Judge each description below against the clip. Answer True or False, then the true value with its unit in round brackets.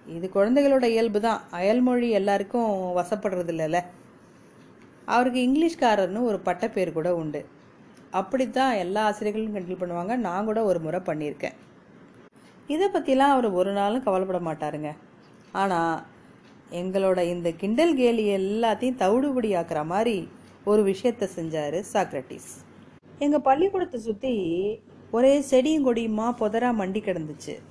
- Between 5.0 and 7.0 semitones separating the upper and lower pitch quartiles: True (5.4 semitones)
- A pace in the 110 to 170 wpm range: True (115 wpm)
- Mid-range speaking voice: False (210 Hz)